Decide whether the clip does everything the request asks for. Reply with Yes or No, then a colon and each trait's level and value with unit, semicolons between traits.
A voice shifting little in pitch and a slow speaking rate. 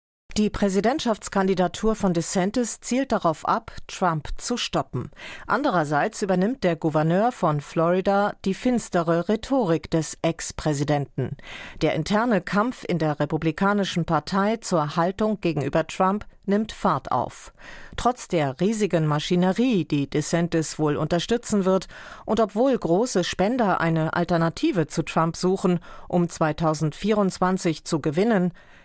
No: average, 4.1 semitones; slow, 120 wpm